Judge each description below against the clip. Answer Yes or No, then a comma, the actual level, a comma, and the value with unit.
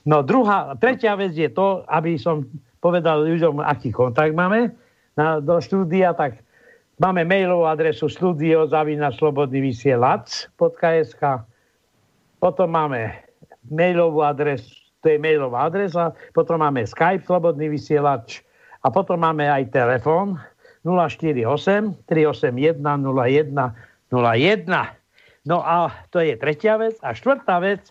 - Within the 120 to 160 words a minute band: No, slow, 110 wpm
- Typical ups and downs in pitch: Yes, average, 3.7 semitones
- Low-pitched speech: No, medium, 160 Hz